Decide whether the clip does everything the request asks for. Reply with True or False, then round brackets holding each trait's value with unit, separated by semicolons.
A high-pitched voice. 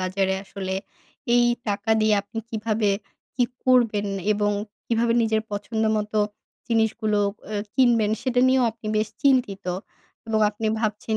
True (220 Hz)